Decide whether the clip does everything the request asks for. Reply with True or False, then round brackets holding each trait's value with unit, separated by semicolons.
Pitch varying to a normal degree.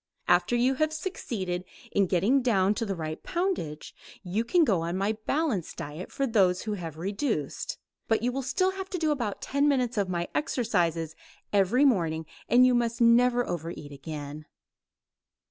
False (7.0 semitones)